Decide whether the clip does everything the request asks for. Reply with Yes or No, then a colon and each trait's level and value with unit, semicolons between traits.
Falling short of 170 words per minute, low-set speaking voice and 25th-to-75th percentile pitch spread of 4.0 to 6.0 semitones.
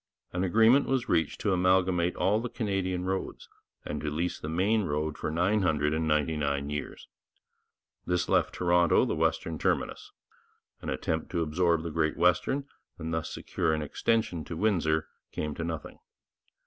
No: average, 150 wpm; very low, 85 Hz; average, 3.1 semitones